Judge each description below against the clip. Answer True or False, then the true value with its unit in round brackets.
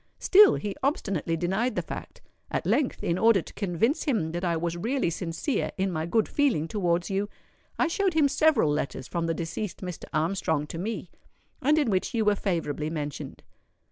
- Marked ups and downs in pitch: True (6.0 semitones)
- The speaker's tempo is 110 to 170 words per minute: False (185 wpm)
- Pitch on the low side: False (190 Hz)